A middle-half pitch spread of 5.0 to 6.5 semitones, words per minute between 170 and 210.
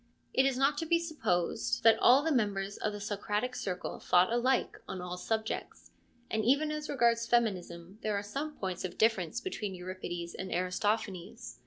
Yes: wide, 5.4 semitones; average, 175 wpm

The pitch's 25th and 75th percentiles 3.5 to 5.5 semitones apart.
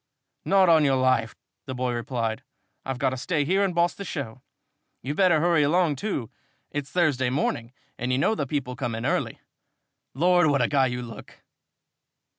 Yes: average, 5.2 semitones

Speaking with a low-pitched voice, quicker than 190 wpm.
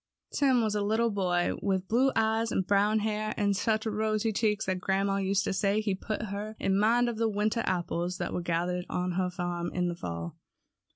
No: high, 200 Hz; fast, 205 wpm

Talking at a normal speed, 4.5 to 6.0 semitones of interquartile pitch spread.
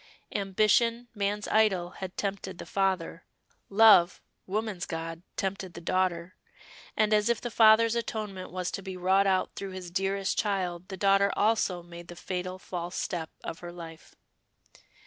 No: average, 155 wpm; average, 2.7 semitones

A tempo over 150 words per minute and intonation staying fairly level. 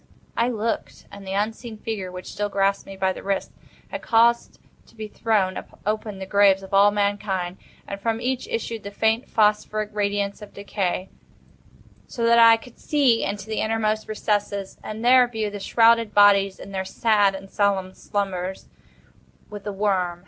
Yes: average, 170 wpm; narrow, 2.3 semitones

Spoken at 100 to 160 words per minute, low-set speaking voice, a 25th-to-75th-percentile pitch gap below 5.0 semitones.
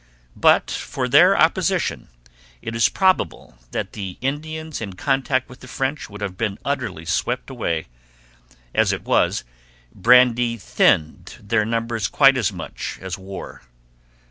No: average, 140 wpm; low, 115 Hz; average, 5.3 semitones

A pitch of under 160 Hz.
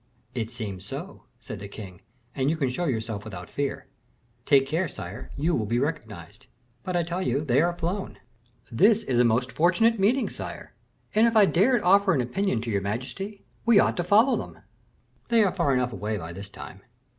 Yes: medium, 140 Hz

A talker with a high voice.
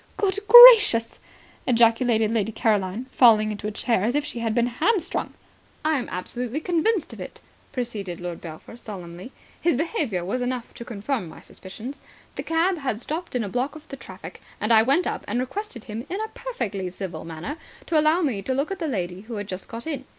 Yes: high, 240 Hz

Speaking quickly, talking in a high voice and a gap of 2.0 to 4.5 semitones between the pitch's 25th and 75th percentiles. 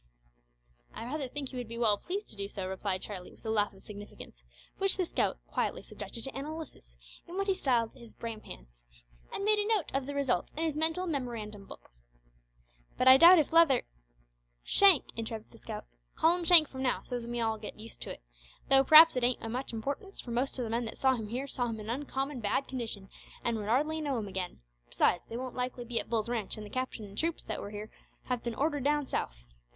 No: fast, 235 wpm; high, 245 Hz; average, 5.1 semitones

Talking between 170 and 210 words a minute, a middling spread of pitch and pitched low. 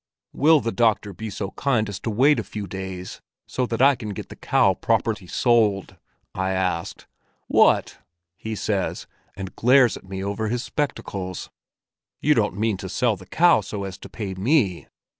Yes: average, 180 wpm; average, 4.1 semitones; low, 105 Hz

